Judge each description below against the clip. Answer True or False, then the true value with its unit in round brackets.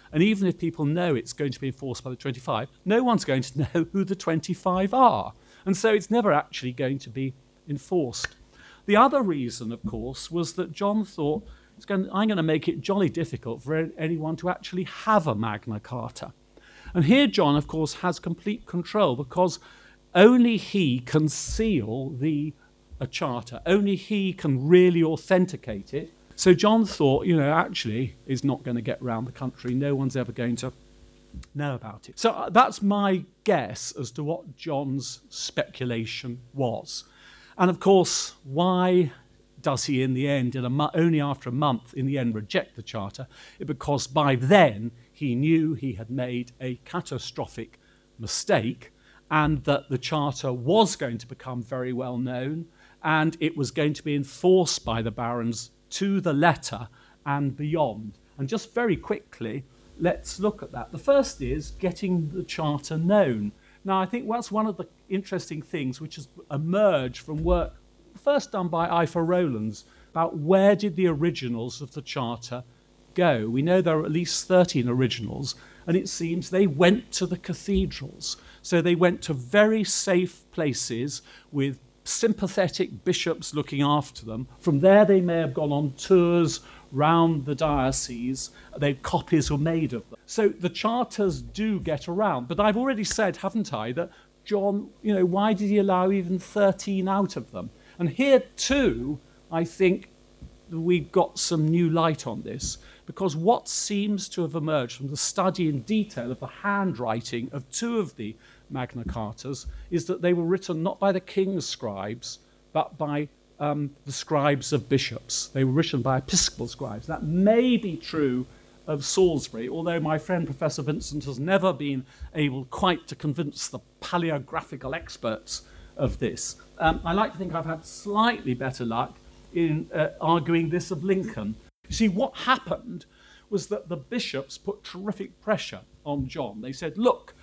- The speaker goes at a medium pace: True (170 wpm)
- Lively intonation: True (6.1 semitones)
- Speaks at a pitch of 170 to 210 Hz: False (155 Hz)